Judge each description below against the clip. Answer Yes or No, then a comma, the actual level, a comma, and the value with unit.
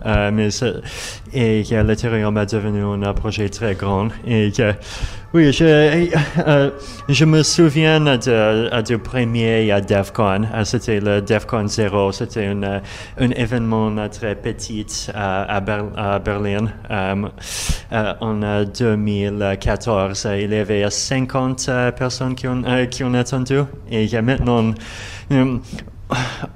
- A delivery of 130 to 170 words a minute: Yes, average, 150 wpm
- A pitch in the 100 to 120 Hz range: Yes, low, 110 Hz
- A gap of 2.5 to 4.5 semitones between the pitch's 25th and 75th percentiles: Yes, average, 3.3 semitones